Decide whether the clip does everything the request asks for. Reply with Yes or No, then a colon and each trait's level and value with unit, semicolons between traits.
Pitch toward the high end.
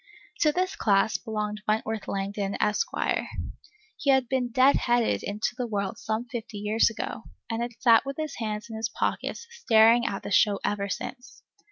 Yes: high, 225 Hz